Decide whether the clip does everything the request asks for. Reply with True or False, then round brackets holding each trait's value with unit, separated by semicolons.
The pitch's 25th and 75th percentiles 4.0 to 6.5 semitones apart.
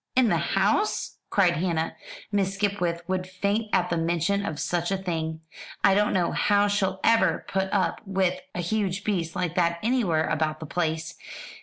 False (3.0 semitones)